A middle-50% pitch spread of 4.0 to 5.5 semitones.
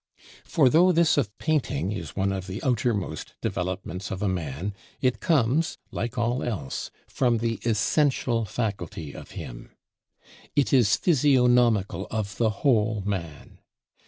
Yes: average, 4.8 semitones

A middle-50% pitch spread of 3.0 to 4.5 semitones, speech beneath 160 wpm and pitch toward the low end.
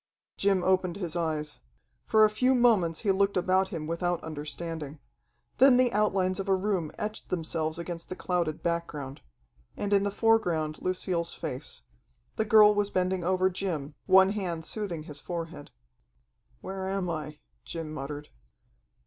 No: average, 3.5 semitones; average, 150 wpm; medium, 180 Hz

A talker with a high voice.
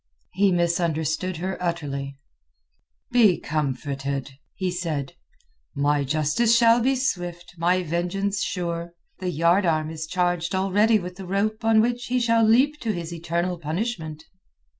No: medium, 175 Hz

